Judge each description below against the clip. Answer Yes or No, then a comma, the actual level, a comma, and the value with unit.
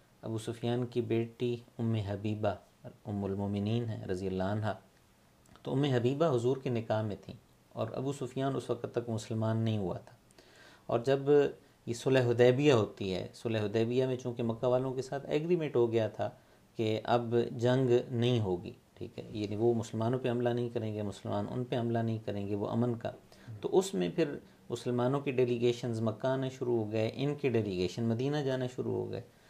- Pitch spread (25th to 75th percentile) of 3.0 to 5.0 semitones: No, narrow, 2.5 semitones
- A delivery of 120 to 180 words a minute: No, fast, 190 wpm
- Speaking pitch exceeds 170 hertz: No, low, 120 Hz